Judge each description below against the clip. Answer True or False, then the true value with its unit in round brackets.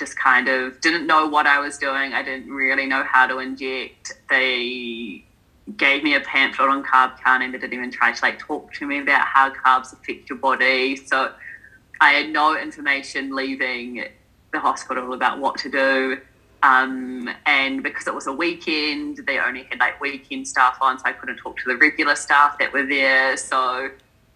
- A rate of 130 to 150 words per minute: False (190 wpm)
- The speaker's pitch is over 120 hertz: True (135 Hz)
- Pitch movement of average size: False (1.8 semitones)